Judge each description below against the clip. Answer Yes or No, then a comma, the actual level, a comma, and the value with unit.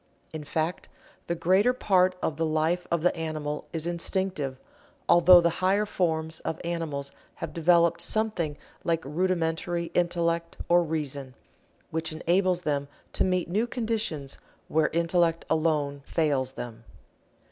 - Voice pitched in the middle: Yes, medium, 165 Hz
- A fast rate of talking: No, slow, 135 wpm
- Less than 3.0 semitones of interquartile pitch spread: Yes, narrow, 2.4 semitones